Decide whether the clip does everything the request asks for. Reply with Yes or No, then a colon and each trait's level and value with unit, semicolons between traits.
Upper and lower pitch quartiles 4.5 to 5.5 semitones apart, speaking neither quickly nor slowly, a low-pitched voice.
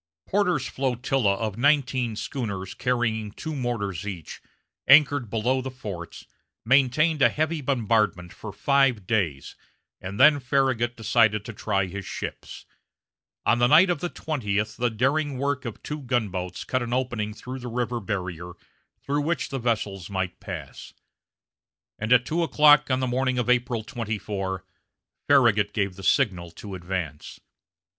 Yes: average, 4.8 semitones; average, 150 wpm; low, 120 Hz